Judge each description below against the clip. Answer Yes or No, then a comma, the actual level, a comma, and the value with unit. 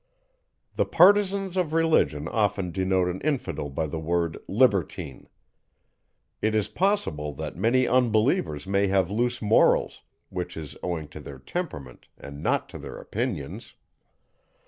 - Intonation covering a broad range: Yes, wide, 8.4 semitones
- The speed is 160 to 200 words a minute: No, average, 140 wpm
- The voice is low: Yes, very low, 95 Hz